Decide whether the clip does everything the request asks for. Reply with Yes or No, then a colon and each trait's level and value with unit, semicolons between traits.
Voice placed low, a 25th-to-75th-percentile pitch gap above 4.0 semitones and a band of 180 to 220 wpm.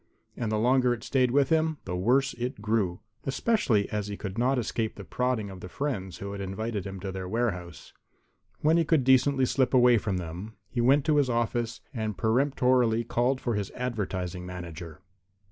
Yes: low, 115 Hz; average, 4.7 semitones; average, 190 wpm